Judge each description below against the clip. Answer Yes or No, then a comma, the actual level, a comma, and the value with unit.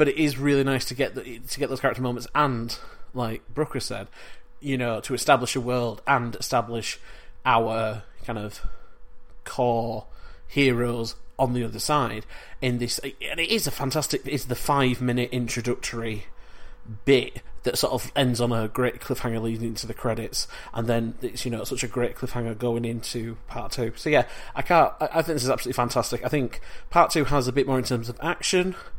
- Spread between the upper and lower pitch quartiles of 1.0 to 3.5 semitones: Yes, average, 2.9 semitones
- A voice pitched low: Yes, low, 125 Hz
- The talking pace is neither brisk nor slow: Yes, average, 195 wpm